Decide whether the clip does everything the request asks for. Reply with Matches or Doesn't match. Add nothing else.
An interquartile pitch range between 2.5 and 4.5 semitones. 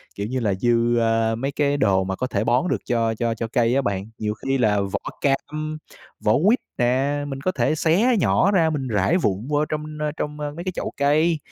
Doesn't match